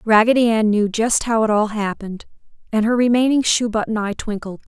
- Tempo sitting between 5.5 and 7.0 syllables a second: Yes, 5.6 syllables/s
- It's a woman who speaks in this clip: Yes, female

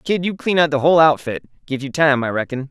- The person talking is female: No, male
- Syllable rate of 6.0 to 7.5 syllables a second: Yes, 6.2 syllables/s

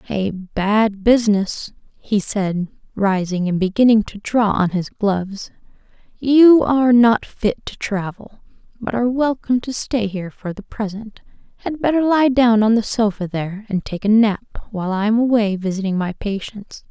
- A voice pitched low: No, high, 215 Hz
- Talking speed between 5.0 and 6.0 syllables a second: No, 4.6 syllables/s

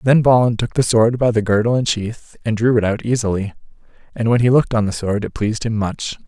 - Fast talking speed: Yes, fast, 250 wpm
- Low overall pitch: Yes, low, 115 Hz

